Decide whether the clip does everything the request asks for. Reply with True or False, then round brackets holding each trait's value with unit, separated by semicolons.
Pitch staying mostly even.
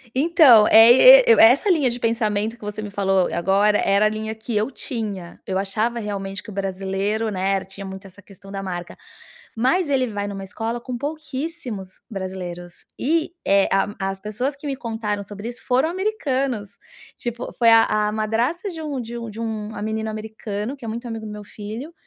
False (3.8 semitones)